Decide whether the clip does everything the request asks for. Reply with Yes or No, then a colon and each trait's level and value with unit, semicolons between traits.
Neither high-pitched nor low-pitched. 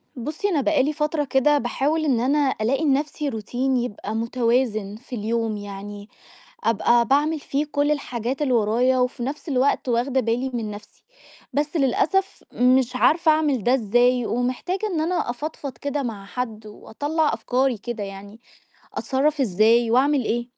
No: very high, 255 Hz